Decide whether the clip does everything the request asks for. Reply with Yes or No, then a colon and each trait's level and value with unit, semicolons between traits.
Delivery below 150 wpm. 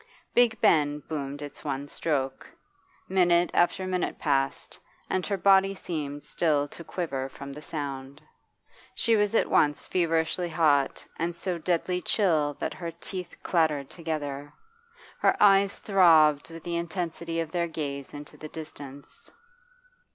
Yes: average, 140 wpm